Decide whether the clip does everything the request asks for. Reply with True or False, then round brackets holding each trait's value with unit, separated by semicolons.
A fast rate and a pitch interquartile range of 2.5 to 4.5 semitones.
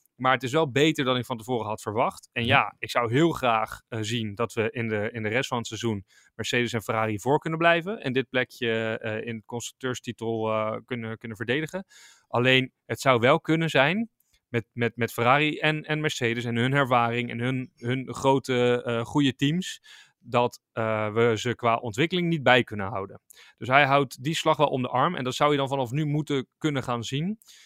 True (215 wpm; 3.7 semitones)